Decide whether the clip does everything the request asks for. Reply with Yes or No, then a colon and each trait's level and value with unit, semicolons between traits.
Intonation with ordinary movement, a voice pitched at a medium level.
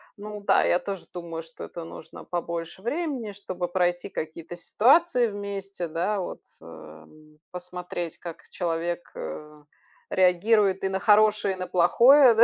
Yes: average, 3.6 semitones; medium, 180 Hz